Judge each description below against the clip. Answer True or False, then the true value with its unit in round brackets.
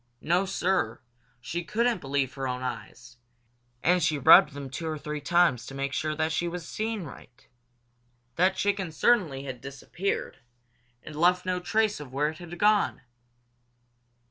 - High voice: False (160 Hz)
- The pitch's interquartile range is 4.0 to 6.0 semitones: True (4.8 semitones)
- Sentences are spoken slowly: False (160 wpm)